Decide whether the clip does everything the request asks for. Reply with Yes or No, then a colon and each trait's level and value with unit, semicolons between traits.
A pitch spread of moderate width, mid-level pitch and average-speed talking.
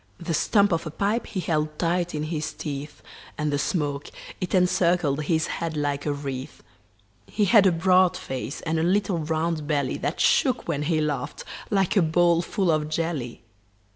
Yes: average, 3.2 semitones; medium, 160 Hz; average, 180 wpm